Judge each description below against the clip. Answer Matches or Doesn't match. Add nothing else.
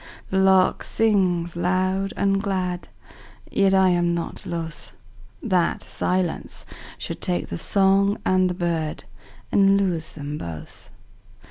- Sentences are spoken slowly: Matches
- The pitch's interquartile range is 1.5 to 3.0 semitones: Matches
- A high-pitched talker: Doesn't match